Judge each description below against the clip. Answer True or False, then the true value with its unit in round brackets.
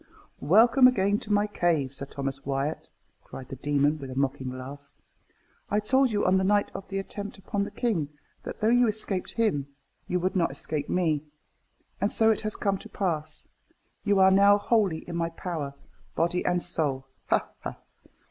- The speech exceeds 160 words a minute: True (185 wpm)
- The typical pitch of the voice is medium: True (180 Hz)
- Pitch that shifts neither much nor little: False (6.1 semitones)